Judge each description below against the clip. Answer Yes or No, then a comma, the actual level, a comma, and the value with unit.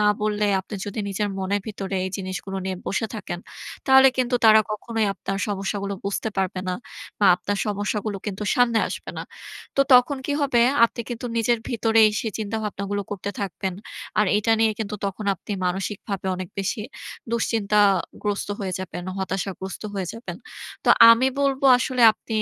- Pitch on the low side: No, high, 205 Hz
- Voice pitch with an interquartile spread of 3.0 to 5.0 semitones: No, narrow, 2.5 semitones